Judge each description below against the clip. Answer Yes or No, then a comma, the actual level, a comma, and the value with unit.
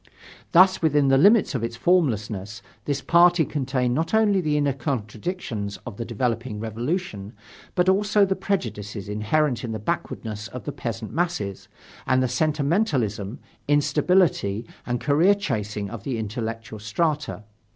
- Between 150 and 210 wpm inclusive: No, average, 140 wpm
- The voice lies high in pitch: No, low, 130 Hz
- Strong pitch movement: Yes, wide, 7.0 semitones